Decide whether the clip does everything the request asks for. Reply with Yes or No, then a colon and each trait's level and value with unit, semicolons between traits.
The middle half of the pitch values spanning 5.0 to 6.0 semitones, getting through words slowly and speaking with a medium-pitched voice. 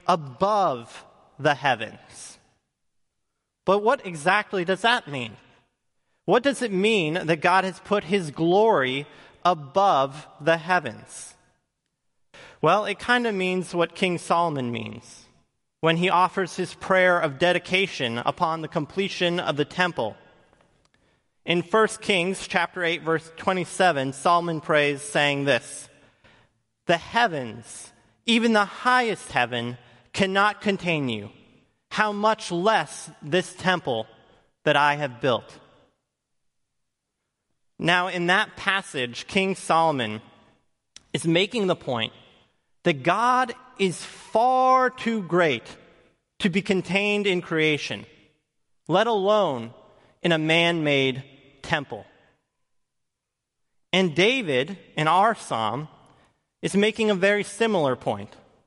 Yes: average, 5.3 semitones; slow, 115 wpm; medium, 175 Hz